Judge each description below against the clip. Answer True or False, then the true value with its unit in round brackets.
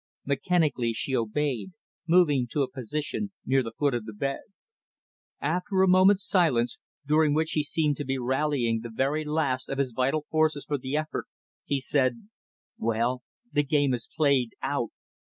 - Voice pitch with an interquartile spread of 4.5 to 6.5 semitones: False (3.5 semitones)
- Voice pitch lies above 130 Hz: True (140 Hz)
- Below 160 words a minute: False (165 wpm)